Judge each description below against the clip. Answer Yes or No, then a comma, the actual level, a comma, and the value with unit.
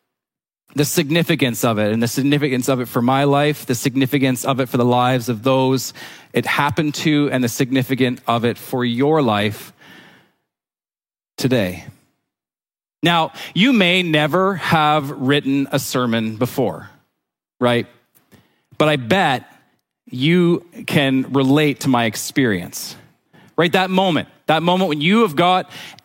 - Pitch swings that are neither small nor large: Yes, average, 3.8 semitones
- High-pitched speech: No, medium, 140 Hz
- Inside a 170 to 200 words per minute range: No, average, 140 wpm